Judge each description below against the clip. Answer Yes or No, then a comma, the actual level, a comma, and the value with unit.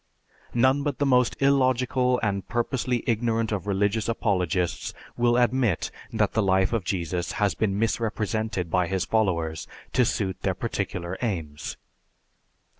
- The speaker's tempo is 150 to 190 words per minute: No, slow, 135 wpm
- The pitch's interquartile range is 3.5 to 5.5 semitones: Yes, average, 4.3 semitones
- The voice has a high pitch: No, low, 110 Hz